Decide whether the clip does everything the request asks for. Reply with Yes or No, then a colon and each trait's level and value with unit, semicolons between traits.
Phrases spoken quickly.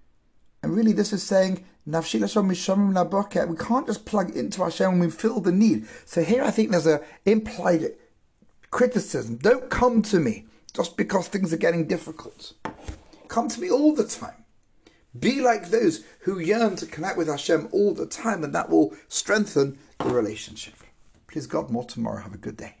No: average, 175 wpm